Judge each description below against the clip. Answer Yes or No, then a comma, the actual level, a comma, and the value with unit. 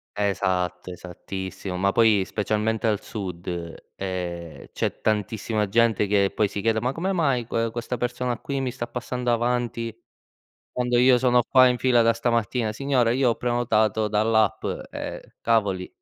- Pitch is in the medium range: No, low, 115 Hz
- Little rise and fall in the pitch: No, average, 3.3 semitones